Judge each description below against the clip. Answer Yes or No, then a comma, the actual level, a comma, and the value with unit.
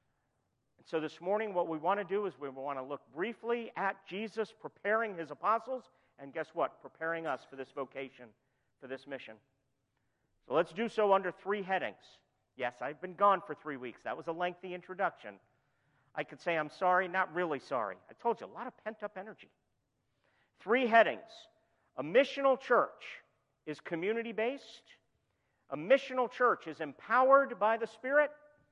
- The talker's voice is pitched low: No, medium, 180 Hz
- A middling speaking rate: Yes, average, 170 wpm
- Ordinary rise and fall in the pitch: No, wide, 8.3 semitones